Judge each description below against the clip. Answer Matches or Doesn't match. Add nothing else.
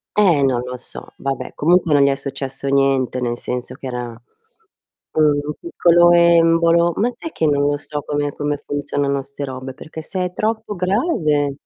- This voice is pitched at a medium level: Matches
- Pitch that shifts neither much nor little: Matches